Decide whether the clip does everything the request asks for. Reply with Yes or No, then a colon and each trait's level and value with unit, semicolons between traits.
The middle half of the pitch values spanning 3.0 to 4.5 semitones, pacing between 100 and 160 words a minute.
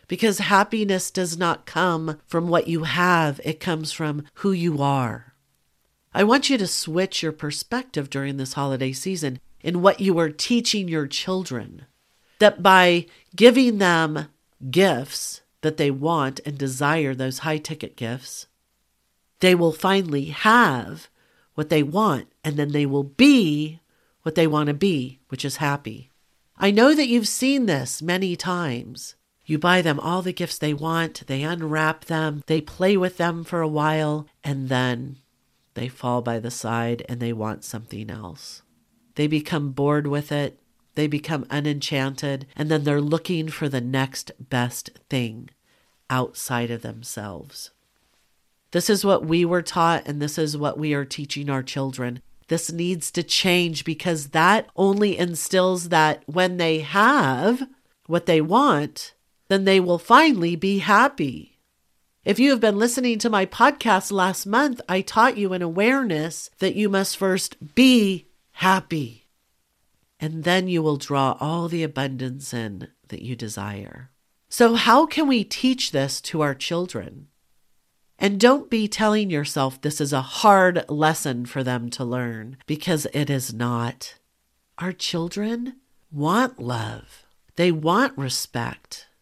No: wide, 5.6 semitones; average, 155 wpm